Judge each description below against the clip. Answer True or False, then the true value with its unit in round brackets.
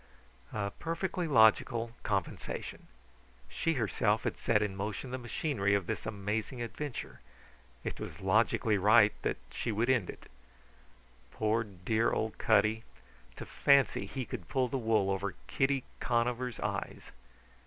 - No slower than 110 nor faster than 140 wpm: True (135 wpm)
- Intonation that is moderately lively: True (3.8 semitones)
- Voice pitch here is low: True (110 Hz)